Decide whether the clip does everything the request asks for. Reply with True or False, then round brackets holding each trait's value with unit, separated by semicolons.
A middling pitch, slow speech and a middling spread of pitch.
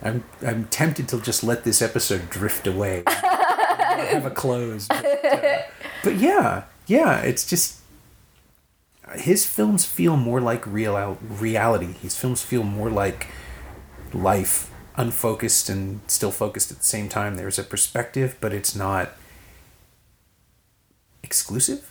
False (105 Hz; 130 wpm; 3.8 semitones)